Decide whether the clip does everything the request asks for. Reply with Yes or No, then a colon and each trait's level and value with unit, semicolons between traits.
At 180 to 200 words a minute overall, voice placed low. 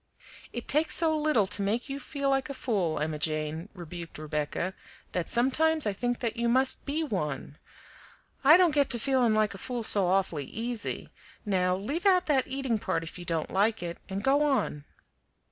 No: average, 190 wpm; high, 225 Hz